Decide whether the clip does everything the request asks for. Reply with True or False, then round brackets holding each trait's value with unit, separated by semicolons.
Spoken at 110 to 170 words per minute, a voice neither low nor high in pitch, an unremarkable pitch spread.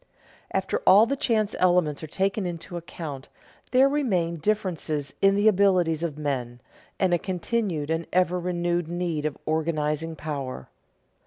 True (150 wpm; 175 Hz; 3.8 semitones)